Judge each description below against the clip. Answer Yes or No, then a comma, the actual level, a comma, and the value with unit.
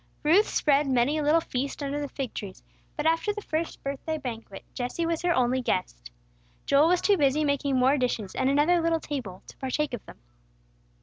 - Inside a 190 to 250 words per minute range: Yes, average, 195 wpm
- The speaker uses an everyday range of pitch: Yes, average, 3.8 semitones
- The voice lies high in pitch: Yes, very high, 285 Hz